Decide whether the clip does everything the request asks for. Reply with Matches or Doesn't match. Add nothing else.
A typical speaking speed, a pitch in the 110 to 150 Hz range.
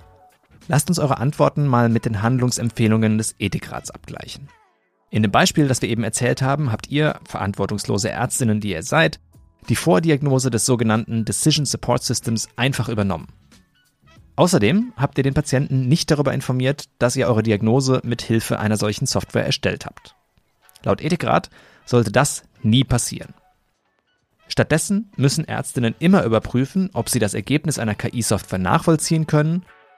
Matches